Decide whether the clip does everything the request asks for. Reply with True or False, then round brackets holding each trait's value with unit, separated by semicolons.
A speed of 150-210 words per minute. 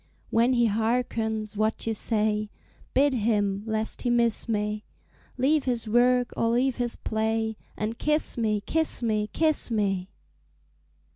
False (140 wpm)